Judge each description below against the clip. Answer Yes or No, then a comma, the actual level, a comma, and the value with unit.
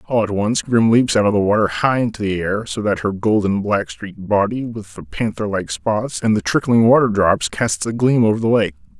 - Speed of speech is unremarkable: No, fast, 240 wpm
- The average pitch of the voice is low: Yes, low, 105 Hz